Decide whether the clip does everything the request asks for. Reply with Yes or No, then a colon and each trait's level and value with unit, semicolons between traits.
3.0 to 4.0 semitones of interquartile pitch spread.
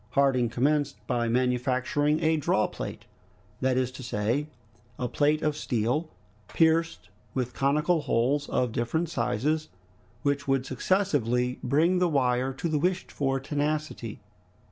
Yes: average, 3.6 semitones